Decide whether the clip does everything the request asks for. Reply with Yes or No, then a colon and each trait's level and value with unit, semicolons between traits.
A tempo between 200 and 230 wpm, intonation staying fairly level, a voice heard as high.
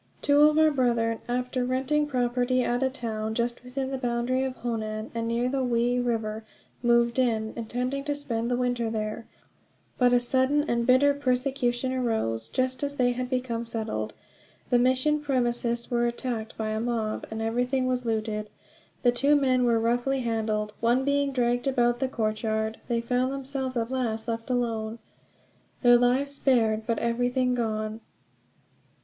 No: average, 165 wpm; narrow, 2.1 semitones; high, 245 Hz